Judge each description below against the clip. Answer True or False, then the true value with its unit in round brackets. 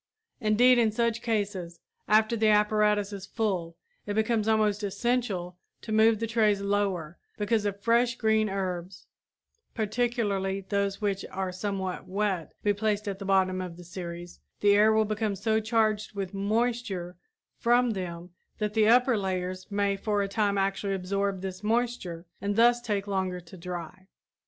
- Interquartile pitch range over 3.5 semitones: False (2.5 semitones)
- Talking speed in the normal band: True (160 wpm)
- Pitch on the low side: False (205 Hz)